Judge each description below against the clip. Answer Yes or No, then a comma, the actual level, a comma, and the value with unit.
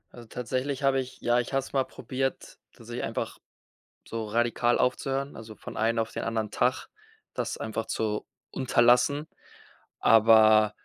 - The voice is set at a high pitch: No, low, 120 Hz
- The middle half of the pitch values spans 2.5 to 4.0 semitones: Yes, average, 2.9 semitones